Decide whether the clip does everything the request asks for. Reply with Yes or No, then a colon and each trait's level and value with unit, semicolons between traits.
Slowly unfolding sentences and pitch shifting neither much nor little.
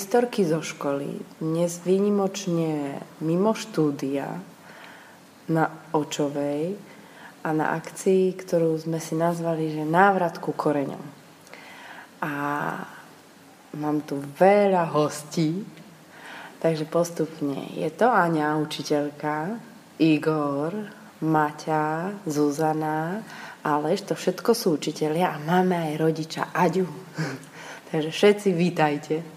Yes: slow, 95 wpm; average, 3.2 semitones